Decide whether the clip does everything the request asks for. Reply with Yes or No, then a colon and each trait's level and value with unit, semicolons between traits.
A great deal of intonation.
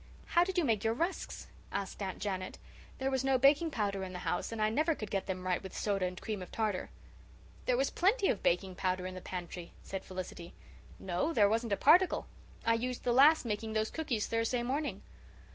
Yes: wide, 6.2 semitones